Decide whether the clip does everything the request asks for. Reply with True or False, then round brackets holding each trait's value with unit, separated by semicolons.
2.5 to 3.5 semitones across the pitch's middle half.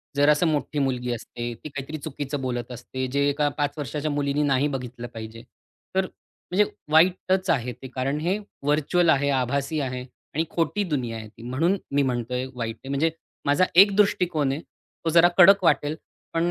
False (4.0 semitones)